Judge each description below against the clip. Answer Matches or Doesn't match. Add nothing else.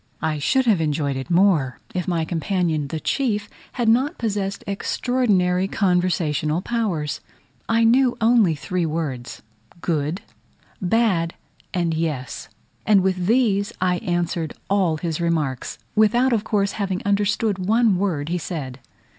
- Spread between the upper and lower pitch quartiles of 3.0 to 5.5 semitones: Matches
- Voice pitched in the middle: Matches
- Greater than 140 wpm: Doesn't match